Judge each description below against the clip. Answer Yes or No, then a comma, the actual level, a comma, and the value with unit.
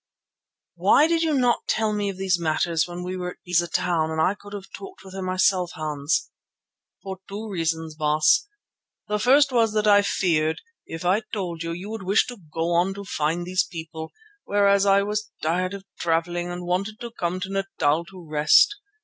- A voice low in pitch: No, medium, 185 Hz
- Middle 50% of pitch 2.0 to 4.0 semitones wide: Yes, average, 3.4 semitones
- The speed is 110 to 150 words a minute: No, average, 195 wpm